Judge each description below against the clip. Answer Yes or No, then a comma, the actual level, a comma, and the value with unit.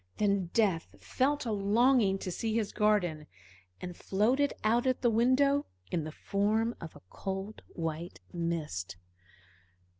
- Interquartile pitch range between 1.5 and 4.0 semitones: No, average, 5.2 semitones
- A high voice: Yes, high, 205 Hz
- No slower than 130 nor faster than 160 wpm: Yes, average, 140 wpm